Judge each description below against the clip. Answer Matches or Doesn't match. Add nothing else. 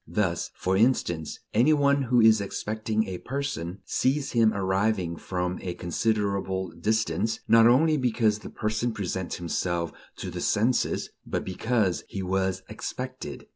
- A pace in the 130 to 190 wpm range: Matches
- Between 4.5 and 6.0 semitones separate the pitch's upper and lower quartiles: Doesn't match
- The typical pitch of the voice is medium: Doesn't match